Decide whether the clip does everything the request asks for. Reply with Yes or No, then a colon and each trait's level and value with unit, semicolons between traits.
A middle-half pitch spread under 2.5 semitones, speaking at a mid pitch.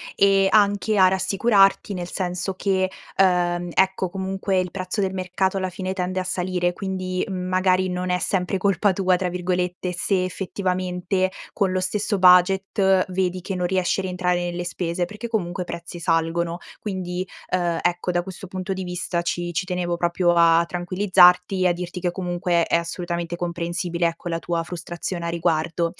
Yes: narrow, 1.4 semitones; medium, 180 Hz